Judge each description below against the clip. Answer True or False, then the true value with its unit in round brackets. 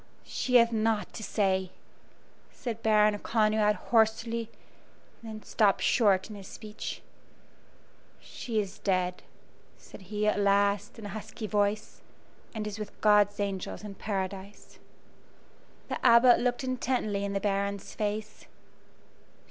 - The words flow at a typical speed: False (130 wpm)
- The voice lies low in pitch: False (210 Hz)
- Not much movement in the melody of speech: True (1.6 semitones)